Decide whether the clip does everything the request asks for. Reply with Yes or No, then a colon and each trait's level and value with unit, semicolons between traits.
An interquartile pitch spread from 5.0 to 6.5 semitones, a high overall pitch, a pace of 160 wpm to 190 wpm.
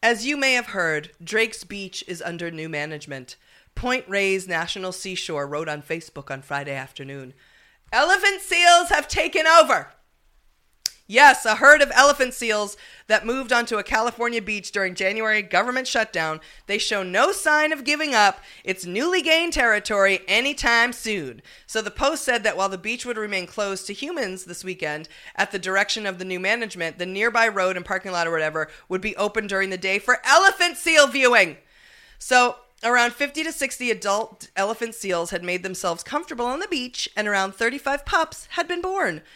Yes: average, 5.3 semitones; high, 210 Hz; average, 180 wpm